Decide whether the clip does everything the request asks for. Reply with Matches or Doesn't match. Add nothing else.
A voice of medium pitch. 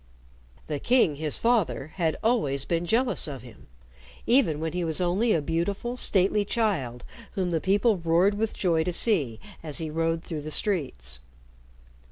Matches